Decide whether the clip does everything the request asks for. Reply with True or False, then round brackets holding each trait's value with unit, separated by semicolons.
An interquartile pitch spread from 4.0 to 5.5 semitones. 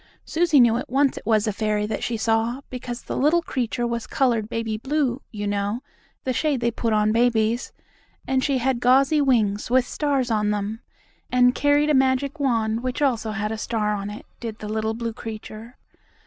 False (3.2 semitones)